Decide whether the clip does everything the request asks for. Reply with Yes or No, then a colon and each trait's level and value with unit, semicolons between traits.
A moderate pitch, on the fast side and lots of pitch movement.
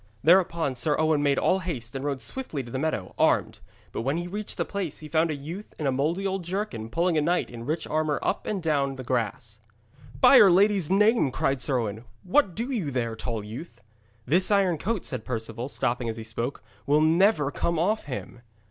Yes: medium, 150 Hz; fast, 210 wpm; wide, 6.4 semitones